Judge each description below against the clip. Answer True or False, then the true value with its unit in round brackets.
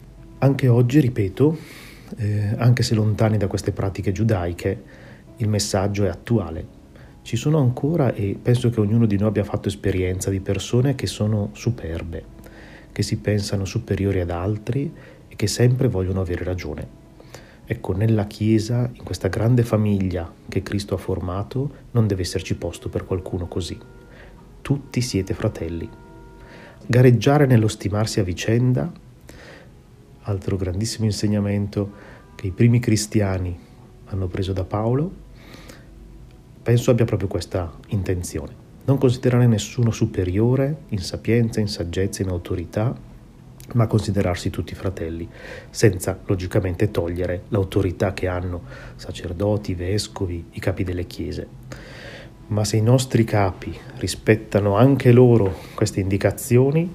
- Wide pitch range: False (3.6 semitones)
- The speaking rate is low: False (130 wpm)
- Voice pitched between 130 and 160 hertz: False (105 Hz)